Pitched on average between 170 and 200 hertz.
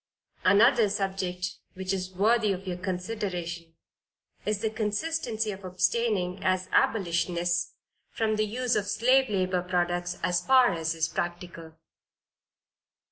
Yes: medium, 185 Hz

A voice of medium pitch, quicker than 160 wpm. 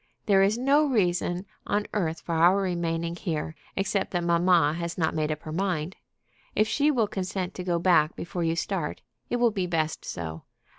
Yes: medium, 175 Hz; average, 190 wpm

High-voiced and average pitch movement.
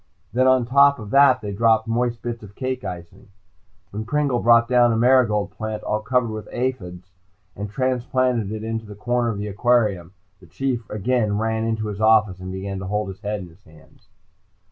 No: low, 110 Hz; average, 3.2 semitones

